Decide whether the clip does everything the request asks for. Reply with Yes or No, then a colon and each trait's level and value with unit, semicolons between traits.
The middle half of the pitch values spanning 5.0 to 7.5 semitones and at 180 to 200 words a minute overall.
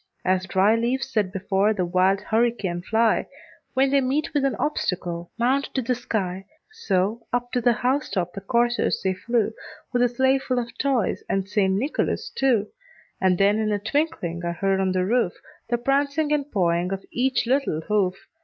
Yes: wide, 5.4 semitones; average, 185 wpm